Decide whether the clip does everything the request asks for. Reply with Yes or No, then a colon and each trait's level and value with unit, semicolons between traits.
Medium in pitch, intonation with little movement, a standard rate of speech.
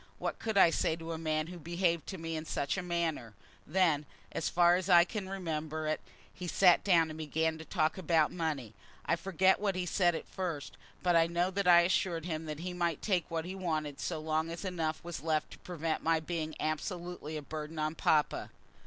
No: medium, 165 Hz; narrow, 2.2 semitones; fast, 215 wpm